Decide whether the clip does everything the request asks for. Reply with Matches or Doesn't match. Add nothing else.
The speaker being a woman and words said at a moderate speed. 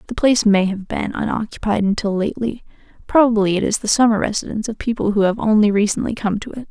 Matches